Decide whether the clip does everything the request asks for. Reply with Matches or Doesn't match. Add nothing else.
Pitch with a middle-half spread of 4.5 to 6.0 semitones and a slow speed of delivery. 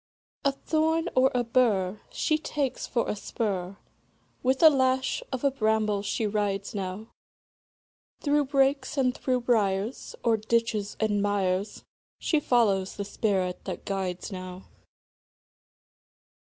Matches